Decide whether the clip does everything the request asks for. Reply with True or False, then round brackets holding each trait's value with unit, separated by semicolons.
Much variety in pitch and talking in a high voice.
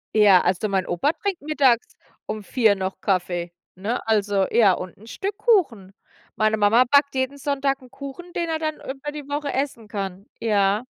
True (6.2 semitones; 230 Hz)